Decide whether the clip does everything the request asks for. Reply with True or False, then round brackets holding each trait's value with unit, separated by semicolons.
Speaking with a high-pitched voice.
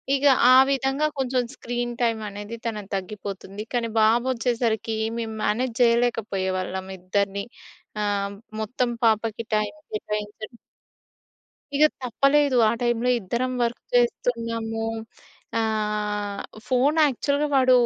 True (230 Hz)